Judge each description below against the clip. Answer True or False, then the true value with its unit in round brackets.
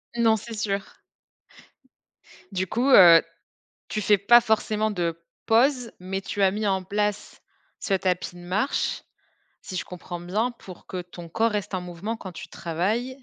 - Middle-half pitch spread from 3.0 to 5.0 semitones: True (3.4 semitones)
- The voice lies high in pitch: True (200 Hz)